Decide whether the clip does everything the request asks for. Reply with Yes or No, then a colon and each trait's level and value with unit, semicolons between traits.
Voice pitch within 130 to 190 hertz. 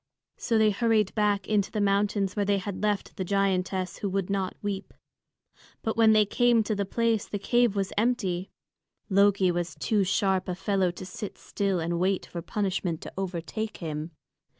No: high, 200 Hz